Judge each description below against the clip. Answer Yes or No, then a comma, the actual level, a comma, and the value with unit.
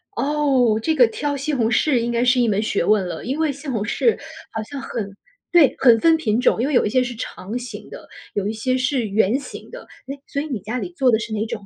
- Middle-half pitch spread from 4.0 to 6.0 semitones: Yes, average, 4.3 semitones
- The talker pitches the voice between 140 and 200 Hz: No, high, 245 Hz